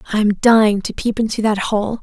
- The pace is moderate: No, fast, 235 wpm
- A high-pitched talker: Yes, high, 215 Hz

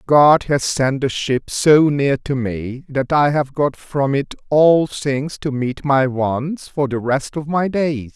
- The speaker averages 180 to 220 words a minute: Yes, average, 200 wpm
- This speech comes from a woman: No, male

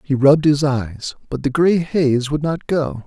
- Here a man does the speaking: Yes, male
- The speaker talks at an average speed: No, fast, 215 wpm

